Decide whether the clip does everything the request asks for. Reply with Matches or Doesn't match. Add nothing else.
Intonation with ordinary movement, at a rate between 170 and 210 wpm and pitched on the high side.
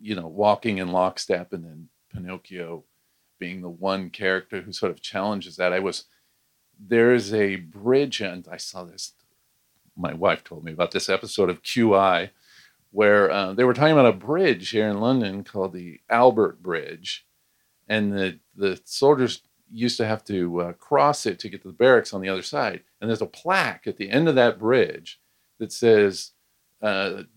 Doesn't match